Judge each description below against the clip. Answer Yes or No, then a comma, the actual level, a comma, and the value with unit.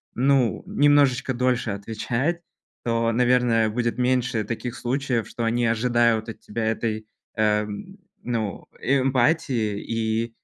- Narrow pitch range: Yes, narrow, 2.2 semitones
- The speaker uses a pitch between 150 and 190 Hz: No, low, 115 Hz